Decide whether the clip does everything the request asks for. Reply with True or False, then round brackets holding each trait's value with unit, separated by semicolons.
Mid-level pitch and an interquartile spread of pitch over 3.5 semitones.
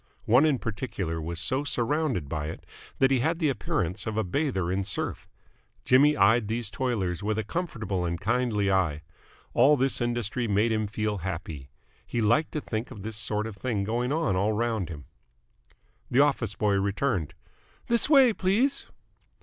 False (110 Hz; 5.3 semitones)